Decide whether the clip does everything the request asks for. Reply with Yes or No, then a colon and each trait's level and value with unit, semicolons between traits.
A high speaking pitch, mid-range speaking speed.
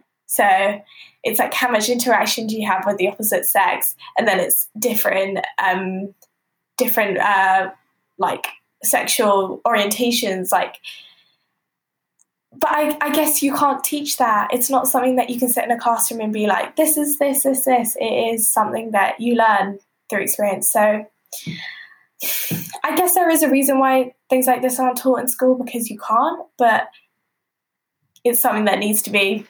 Yes: high, 240 Hz; average, 170 wpm